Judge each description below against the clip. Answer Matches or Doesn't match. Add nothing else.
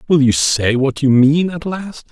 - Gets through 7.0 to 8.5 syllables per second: Doesn't match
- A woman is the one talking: Doesn't match